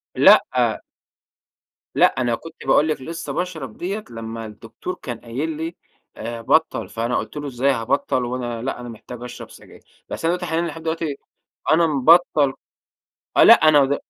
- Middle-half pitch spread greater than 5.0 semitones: Yes, wide, 5.4 semitones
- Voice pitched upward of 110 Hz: Yes, medium, 140 Hz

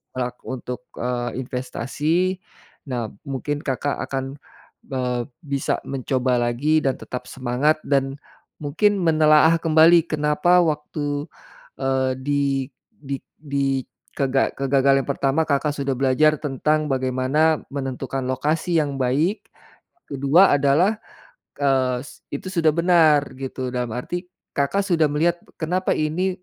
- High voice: No, medium, 140 Hz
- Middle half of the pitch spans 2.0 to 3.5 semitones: Yes, average, 3.0 semitones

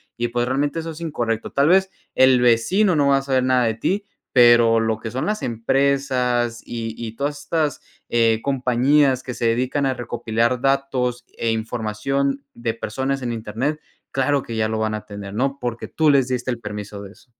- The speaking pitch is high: No, low, 125 Hz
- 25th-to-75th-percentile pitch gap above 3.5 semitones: No, average, 3.2 semitones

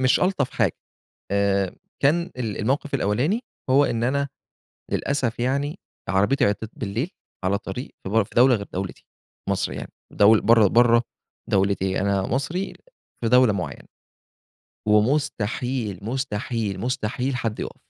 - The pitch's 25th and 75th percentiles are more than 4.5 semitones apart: Yes, average, 4.9 semitones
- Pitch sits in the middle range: No, low, 115 Hz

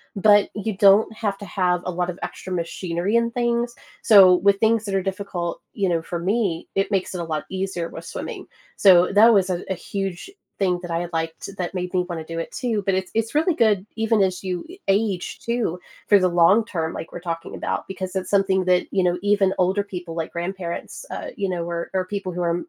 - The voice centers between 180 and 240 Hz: Yes, high, 190 Hz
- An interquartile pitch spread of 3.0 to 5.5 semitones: No, narrow, 2.6 semitones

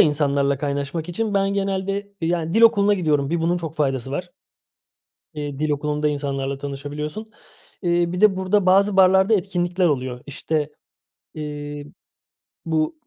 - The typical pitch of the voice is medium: Yes, medium, 160 Hz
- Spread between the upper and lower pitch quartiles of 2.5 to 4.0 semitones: No, average, 4.7 semitones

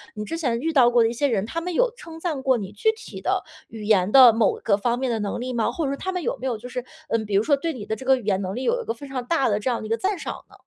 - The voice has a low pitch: No, very high, 250 Hz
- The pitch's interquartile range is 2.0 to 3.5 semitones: No, average, 5.2 semitones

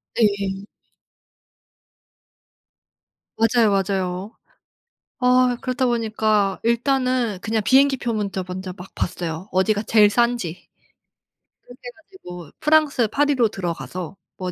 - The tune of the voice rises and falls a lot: No, average, 4.6 semitones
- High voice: Yes, high, 215 Hz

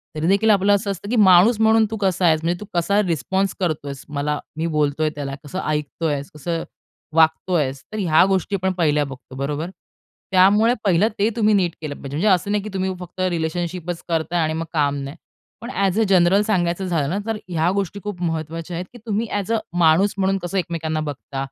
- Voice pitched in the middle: Yes, medium, 175 Hz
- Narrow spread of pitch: No, average, 4.0 semitones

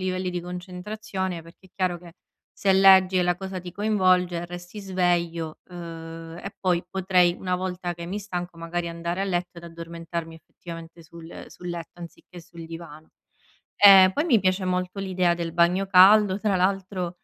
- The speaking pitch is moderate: Yes, medium, 180 Hz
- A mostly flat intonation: Yes, narrow, 1.8 semitones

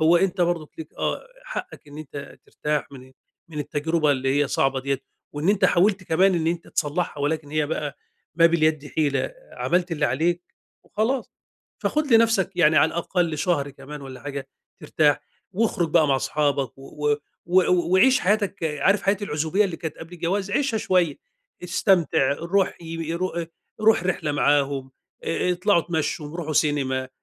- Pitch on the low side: No, medium, 160 Hz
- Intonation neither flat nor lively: Yes, average, 3.8 semitones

